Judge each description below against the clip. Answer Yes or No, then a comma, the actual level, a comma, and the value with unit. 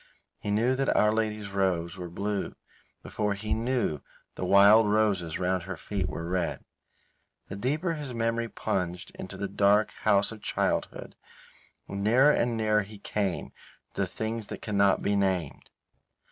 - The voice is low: Yes, low, 105 Hz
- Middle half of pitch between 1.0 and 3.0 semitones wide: Yes, narrow, 2.6 semitones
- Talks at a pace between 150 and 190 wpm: Yes, average, 160 wpm